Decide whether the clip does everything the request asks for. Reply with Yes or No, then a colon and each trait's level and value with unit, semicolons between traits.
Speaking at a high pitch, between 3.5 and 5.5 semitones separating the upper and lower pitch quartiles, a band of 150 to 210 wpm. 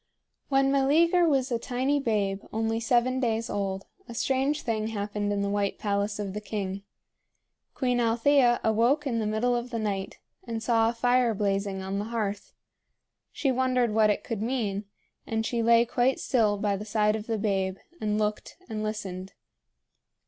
No: high, 225 Hz; average, 3.1 semitones; average, 175 wpm